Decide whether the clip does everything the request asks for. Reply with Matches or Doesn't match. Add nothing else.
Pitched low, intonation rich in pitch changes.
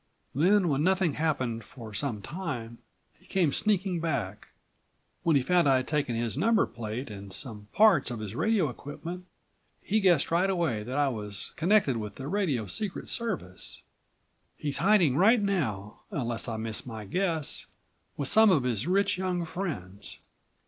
Doesn't match